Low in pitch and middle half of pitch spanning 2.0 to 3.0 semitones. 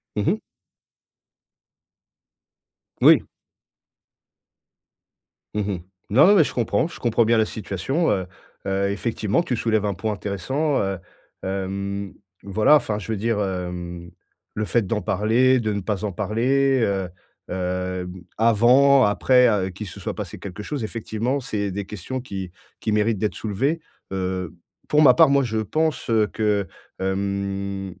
No: low, 105 Hz; average, 3.6 semitones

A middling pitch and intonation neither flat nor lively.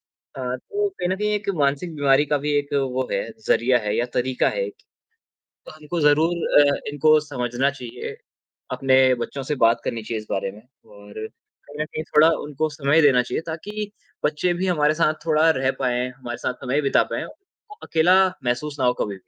Yes: medium, 145 Hz; average, 4.1 semitones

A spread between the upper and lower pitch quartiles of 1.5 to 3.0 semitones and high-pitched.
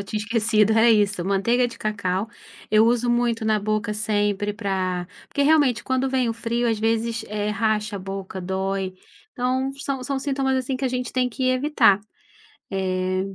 No: average, 3.8 semitones; high, 220 Hz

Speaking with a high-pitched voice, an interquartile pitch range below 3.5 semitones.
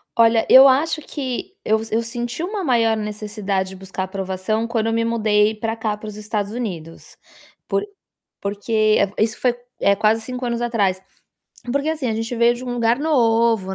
Yes: high, 225 Hz; narrow, 2.5 semitones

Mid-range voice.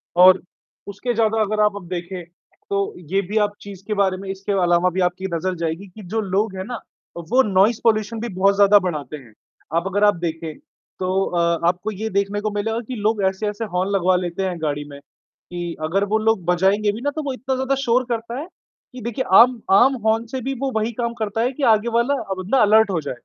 No: high, 200 Hz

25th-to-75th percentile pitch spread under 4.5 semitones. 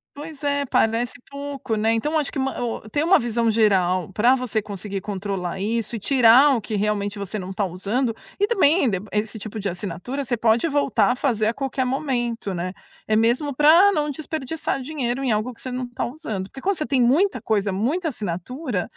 No: average, 5.1 semitones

